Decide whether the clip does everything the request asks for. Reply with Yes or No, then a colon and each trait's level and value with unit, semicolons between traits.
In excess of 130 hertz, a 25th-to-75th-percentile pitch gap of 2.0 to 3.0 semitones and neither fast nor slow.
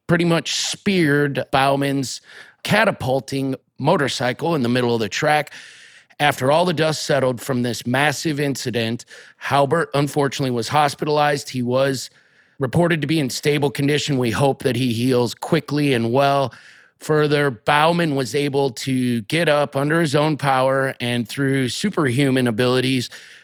Yes: medium, 140 Hz; narrow, 2.6 semitones; average, 145 wpm